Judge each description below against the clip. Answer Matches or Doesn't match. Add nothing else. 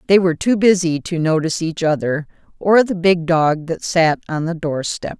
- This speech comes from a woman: Matches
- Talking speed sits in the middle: Doesn't match